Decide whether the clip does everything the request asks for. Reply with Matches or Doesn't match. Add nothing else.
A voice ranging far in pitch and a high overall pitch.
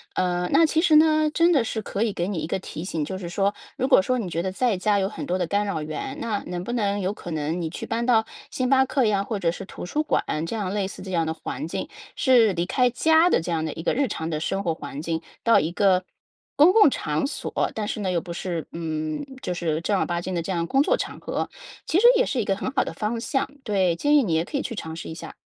Matches